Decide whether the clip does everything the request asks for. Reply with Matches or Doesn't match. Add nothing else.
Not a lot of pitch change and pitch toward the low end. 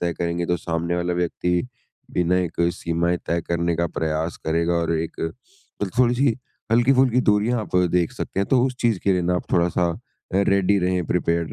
Doesn't match